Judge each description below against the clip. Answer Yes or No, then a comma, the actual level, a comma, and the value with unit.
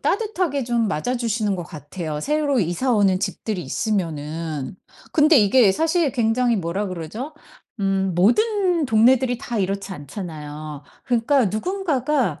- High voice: Yes, high, 220 Hz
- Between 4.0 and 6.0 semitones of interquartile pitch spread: No, wide, 7.0 semitones